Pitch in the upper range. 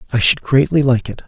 No: low, 125 Hz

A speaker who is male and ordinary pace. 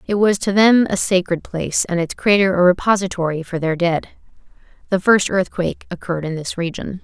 No: female; average, 190 wpm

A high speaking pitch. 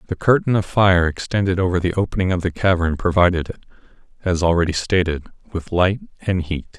No: very low, 90 Hz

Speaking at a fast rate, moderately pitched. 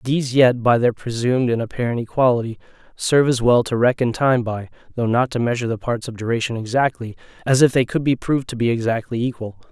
No: fast, 210 wpm; low, 120 Hz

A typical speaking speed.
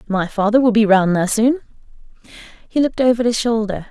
Yes: average, 185 wpm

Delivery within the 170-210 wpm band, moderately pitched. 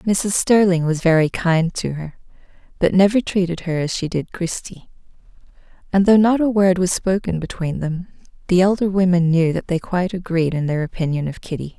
Yes: average, 190 wpm; medium, 180 Hz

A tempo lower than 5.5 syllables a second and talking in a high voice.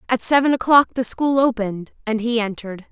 No: 5.8 syllables/s; high, 235 Hz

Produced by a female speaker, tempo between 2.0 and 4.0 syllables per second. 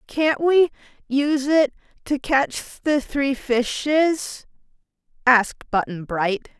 Yes: female; 3.3 syllables/s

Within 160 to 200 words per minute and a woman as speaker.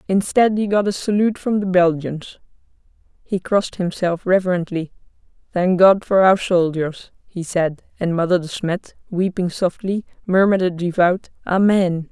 No: average, 145 wpm; female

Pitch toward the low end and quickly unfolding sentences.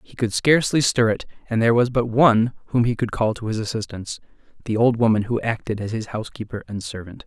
Yes: low, 115 Hz; fast, 215 wpm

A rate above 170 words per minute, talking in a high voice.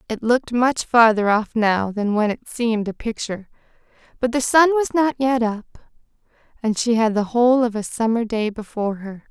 Yes: average, 195 wpm; high, 230 Hz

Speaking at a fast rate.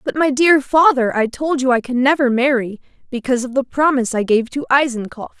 Yes: fast, 210 wpm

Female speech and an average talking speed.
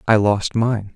No: male; average, 190 wpm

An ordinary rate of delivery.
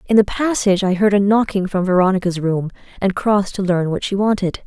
No: fast, 220 wpm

